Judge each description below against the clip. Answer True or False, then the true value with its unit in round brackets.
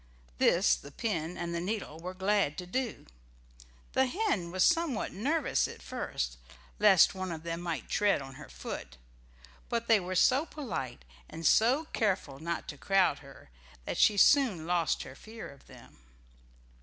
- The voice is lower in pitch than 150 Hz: False (185 Hz)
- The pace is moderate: True (165 wpm)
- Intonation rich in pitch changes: True (5.9 semitones)